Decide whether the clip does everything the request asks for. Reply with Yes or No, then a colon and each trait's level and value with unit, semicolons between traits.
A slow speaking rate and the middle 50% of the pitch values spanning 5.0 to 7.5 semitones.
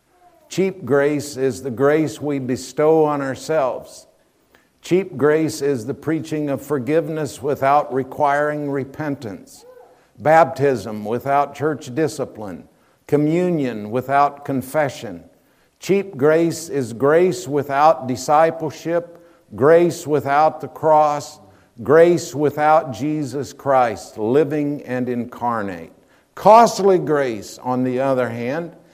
No: slow, 100 wpm; average, 2.9 semitones